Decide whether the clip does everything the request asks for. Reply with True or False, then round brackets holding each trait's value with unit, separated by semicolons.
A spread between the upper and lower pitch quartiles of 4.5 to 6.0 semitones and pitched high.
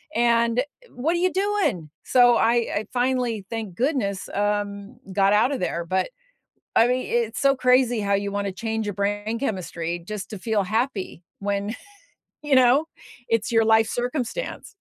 False (3.7 semitones; 225 Hz)